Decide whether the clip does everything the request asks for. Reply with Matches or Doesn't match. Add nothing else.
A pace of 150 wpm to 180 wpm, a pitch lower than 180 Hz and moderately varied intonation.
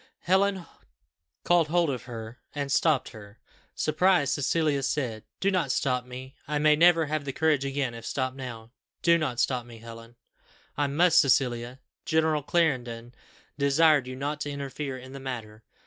Matches